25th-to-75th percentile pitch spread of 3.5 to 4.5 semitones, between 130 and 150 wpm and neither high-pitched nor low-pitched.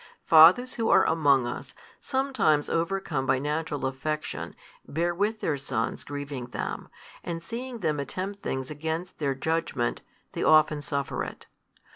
Yes: average, 4.0 semitones; average, 140 wpm; medium, 155 Hz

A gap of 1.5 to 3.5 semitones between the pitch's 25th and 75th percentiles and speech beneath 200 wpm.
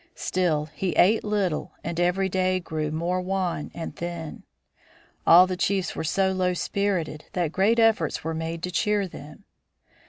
Yes: average, 2.7 semitones; average, 160 wpm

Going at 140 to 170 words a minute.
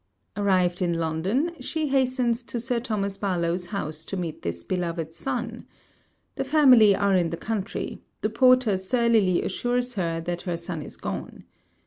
Yes: average, 155 wpm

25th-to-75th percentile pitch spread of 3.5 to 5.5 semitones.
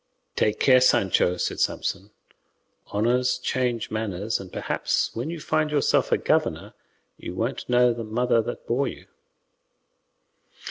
No: average, 2.9 semitones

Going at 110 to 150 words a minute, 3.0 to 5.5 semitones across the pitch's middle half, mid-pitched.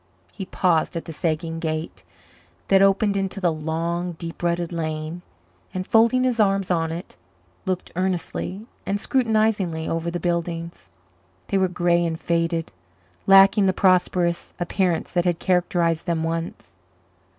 No: average, 140 wpm; narrow, 2.5 semitones; medium, 175 Hz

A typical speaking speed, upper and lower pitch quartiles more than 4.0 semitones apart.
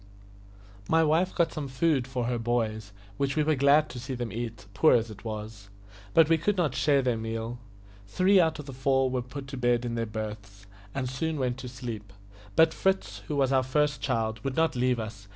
No: fast, 215 wpm; average, 4.6 semitones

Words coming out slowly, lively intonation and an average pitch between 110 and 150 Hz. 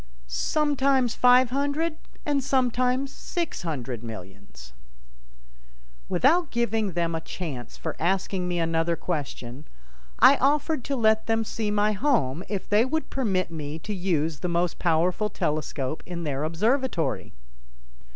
No: slow, 130 wpm; wide, 8.1 semitones; high, 190 Hz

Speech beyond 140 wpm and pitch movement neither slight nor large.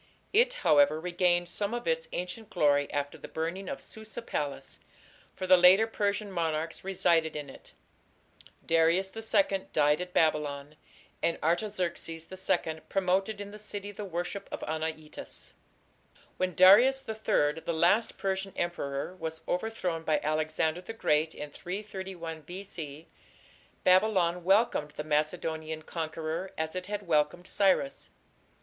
No: slow, 135 wpm; average, 3.8 semitones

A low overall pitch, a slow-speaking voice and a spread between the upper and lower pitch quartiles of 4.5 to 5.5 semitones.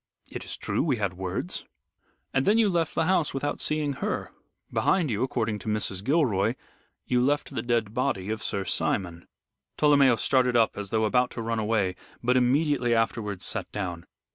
No: low, 120 Hz; average, 180 wpm; average, 5.1 semitones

